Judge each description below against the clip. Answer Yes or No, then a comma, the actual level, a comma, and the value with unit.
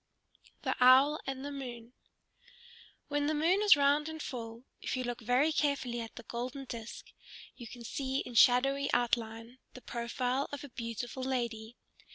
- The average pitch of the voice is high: Yes, very high, 255 Hz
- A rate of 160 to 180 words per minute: Yes, average, 165 wpm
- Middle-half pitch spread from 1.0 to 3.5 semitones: Yes, average, 3.0 semitones